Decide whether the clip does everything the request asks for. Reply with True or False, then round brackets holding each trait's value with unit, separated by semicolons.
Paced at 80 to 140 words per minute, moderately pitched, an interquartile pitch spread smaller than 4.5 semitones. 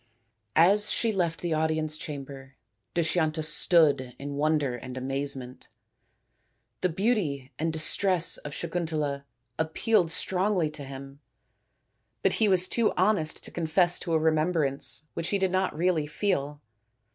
True (135 wpm; 160 Hz; 4.0 semitones)